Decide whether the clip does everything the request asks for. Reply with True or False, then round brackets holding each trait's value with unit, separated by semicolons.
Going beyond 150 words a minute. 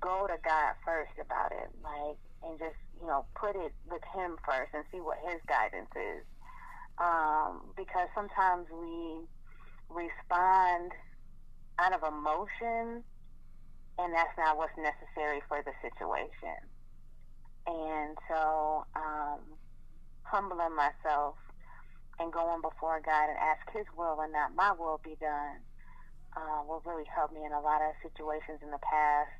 False (145 wpm)